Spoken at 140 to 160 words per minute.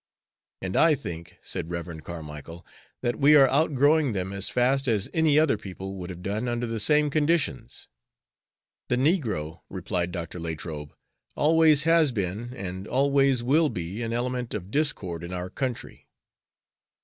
Yes: average, 150 wpm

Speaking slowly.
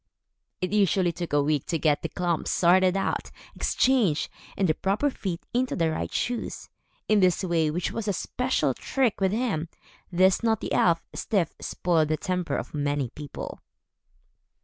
No: average, 165 wpm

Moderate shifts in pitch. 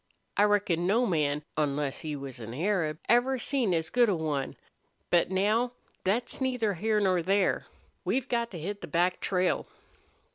No: wide, 5.9 semitones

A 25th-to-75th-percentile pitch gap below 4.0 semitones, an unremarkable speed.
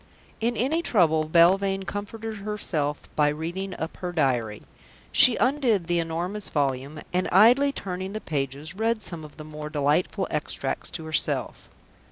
No: wide, 5.5 semitones; average, 150 wpm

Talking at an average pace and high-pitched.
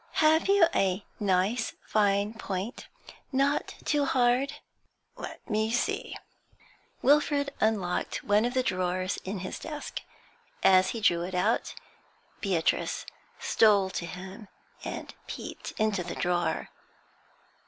No: slow, 120 wpm; high, 210 Hz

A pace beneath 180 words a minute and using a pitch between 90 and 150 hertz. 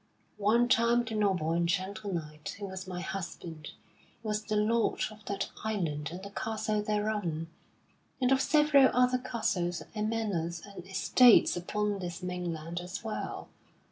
No: average, 150 wpm; high, 200 Hz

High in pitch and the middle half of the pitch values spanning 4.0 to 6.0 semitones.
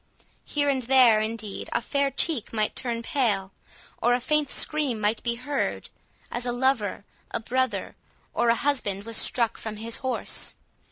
No: high, 240 Hz; average, 3.3 semitones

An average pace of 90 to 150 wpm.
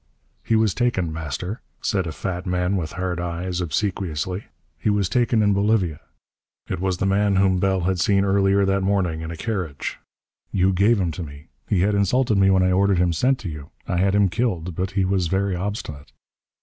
No: average, 200 wpm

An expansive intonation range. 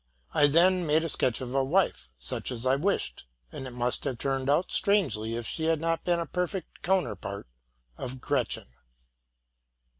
Yes: wide, 5.7 semitones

